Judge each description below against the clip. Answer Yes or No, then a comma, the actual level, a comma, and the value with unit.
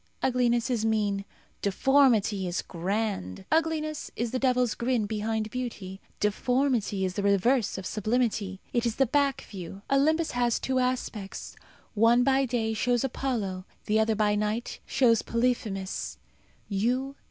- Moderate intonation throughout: Yes, average, 3.7 semitones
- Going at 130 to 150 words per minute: Yes, slow, 135 wpm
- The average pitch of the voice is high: Yes, high, 225 Hz